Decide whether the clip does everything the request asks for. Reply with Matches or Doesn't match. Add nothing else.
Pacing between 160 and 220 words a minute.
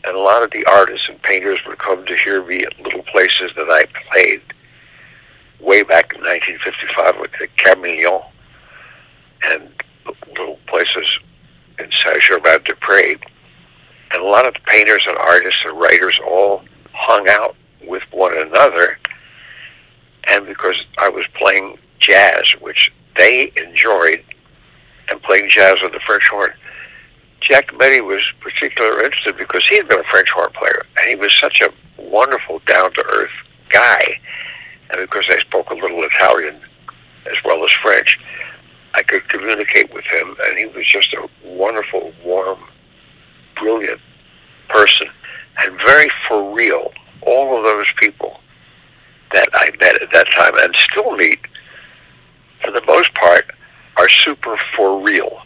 Doesn't match